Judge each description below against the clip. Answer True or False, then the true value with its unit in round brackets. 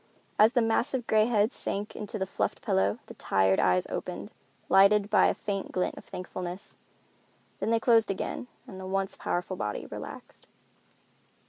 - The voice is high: True (200 Hz)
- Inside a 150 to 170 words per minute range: True (160 wpm)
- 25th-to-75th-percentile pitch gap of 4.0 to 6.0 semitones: False (3.0 semitones)